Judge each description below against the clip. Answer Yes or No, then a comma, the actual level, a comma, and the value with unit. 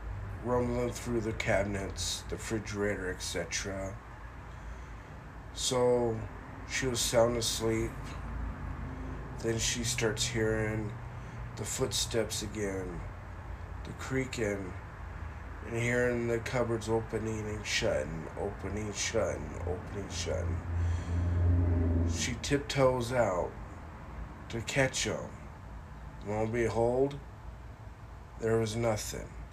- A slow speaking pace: Yes, slow, 90 wpm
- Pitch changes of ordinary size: Yes, average, 4.6 semitones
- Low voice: Yes, low, 105 Hz